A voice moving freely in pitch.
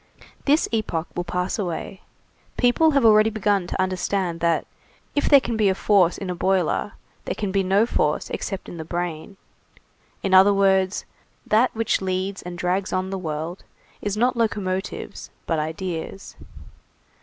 No: average, 2.9 semitones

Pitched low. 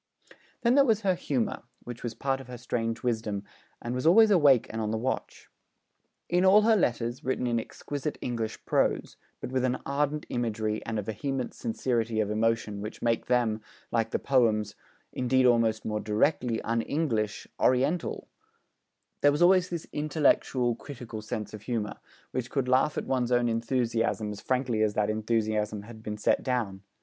Yes: low, 120 Hz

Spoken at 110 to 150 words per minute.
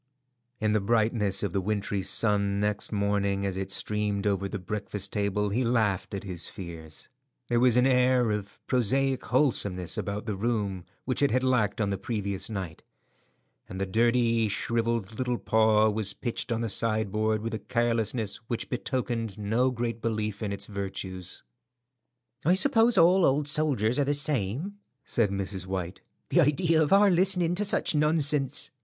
No: average, 165 wpm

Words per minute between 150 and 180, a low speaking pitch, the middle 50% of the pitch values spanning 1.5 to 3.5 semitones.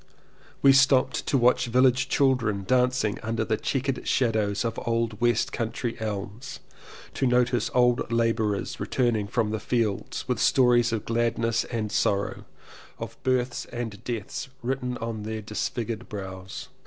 No: average, 140 wpm; low, 115 Hz; narrow, 2.5 semitones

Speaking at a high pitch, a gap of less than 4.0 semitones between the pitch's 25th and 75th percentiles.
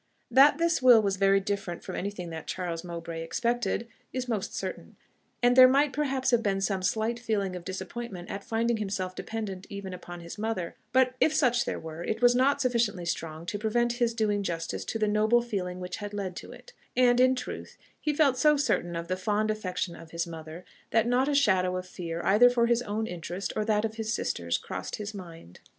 No: high, 210 Hz; average, 4.8 semitones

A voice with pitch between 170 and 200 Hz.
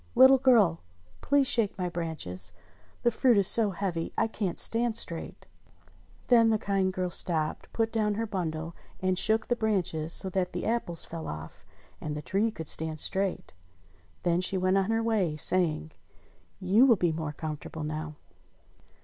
Yes: medium, 185 Hz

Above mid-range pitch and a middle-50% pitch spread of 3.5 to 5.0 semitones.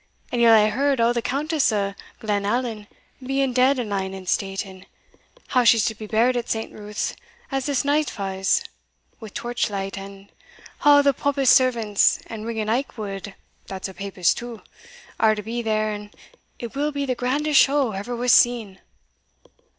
Yes: high, 230 Hz; average, 3.9 semitones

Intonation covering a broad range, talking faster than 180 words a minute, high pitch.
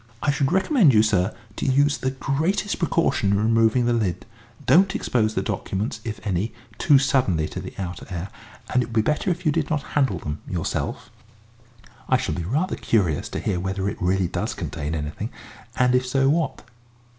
No: wide, 7.0 semitones; average, 190 wpm; low, 115 Hz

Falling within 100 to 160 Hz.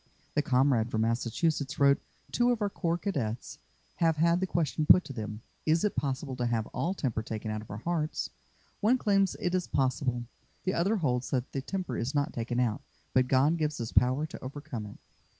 Yes: medium, 140 Hz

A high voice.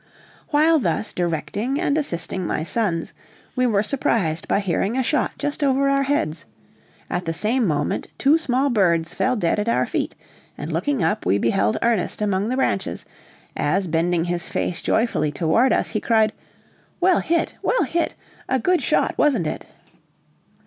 Yes: high, 215 Hz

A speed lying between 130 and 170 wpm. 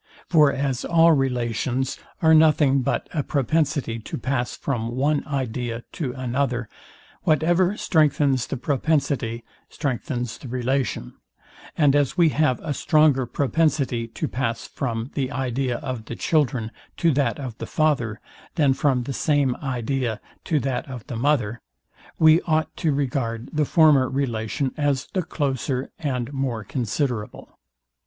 Yes: average, 140 wpm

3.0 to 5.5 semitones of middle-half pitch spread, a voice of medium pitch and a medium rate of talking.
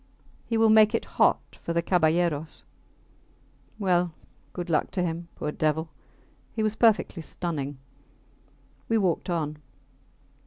No: average, 4.6 semitones; medium, 175 Hz; slow, 125 wpm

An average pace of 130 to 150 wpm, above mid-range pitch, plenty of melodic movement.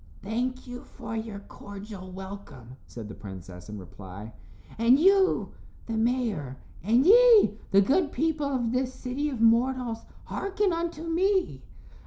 Yes: average, 140 wpm; high, 235 Hz; wide, 7.4 semitones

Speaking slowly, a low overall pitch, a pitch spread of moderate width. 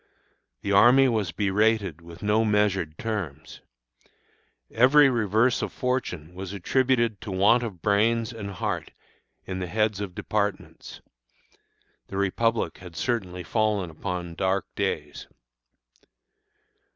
Yes: slow, 120 wpm; low, 100 Hz; average, 3.6 semitones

